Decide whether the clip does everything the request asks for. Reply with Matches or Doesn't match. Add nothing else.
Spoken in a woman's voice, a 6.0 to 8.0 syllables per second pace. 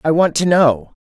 Doesn't match